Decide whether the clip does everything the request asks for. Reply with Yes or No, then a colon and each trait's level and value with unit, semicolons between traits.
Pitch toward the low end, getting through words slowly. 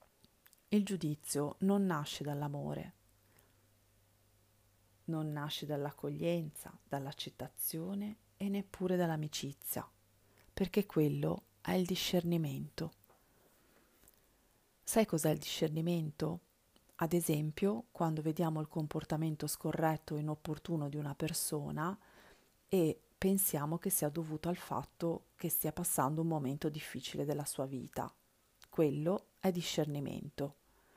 No: medium, 155 Hz; slow, 100 wpm